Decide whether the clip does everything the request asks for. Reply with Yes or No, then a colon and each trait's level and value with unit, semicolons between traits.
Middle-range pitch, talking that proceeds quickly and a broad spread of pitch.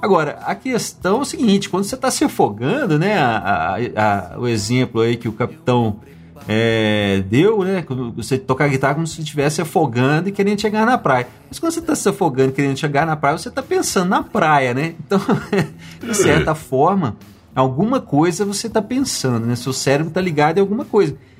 Yes: medium, 155 Hz; fast, 200 wpm; wide, 8.4 semitones